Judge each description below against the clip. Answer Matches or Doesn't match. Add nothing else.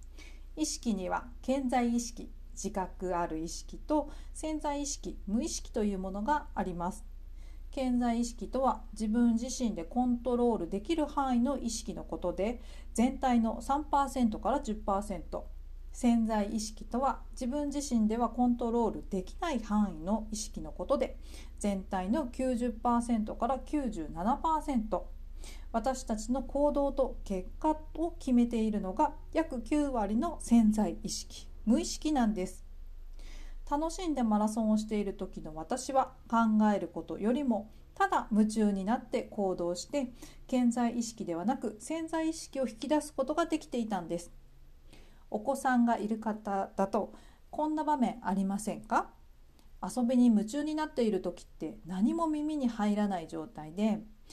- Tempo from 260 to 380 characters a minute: Matches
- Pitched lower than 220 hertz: Doesn't match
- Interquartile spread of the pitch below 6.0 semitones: Matches